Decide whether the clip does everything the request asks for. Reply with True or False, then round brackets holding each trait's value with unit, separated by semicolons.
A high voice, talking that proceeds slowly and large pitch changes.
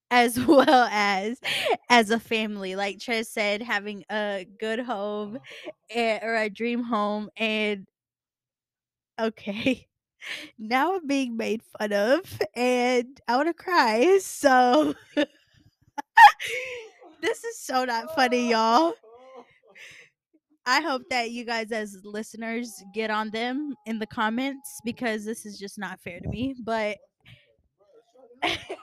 False (230 Hz; 125 wpm; 3.8 semitones)